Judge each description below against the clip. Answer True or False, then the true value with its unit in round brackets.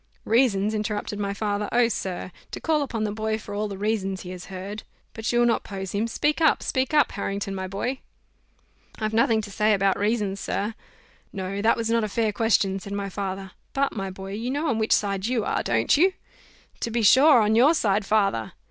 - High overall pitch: True (210 Hz)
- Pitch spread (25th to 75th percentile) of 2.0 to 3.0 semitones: True (2.7 semitones)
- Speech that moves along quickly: True (210 wpm)